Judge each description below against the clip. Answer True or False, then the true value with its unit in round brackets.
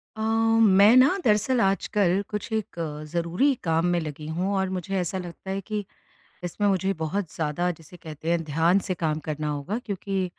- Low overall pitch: False (185 Hz)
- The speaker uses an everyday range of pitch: True (3.9 semitones)